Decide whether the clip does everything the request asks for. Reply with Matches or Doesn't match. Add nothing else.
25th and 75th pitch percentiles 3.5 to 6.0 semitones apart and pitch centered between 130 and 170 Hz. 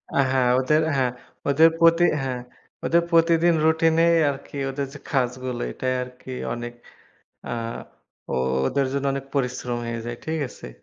Matches